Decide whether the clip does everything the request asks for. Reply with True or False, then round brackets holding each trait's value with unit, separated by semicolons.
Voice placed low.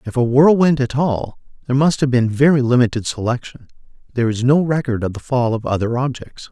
True (125 Hz)